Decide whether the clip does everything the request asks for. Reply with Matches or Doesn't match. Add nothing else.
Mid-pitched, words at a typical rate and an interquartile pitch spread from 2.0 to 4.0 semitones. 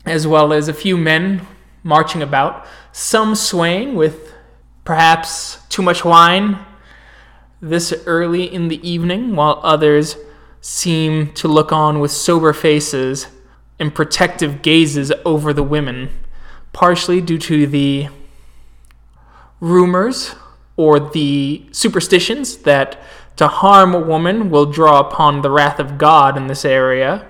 Doesn't match